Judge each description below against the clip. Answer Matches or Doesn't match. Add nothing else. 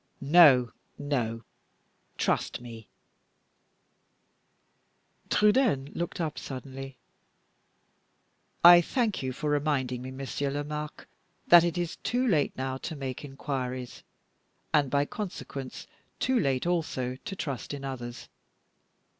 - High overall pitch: Doesn't match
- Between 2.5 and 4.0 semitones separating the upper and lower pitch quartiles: Doesn't match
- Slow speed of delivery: Matches